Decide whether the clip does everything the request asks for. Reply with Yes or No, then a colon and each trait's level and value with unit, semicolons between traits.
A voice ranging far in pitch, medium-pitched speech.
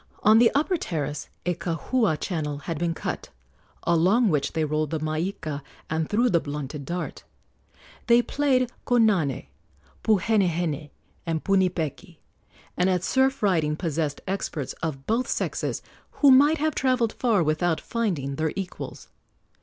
Yes: wide, 6.5 semitones; medium, 175 Hz